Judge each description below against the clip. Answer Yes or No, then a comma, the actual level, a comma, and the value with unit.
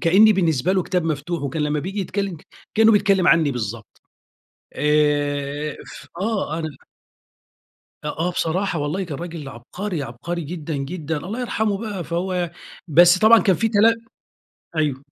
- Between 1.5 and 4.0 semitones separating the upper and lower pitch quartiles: No, average, 4.7 semitones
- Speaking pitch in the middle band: Yes, medium, 170 Hz